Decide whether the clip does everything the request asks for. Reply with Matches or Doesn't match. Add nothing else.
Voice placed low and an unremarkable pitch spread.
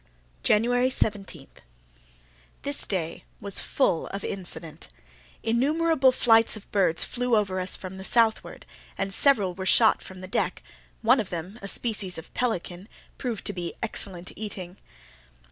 Doesn't match